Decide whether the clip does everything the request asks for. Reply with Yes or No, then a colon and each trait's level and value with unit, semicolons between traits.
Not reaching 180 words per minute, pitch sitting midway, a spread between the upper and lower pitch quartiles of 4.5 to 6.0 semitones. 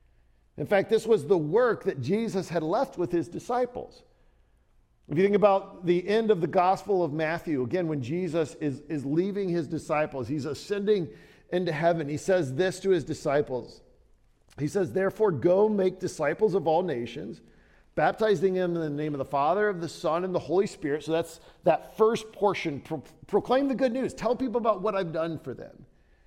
No: average, 190 wpm; medium, 175 Hz; average, 4.8 semitones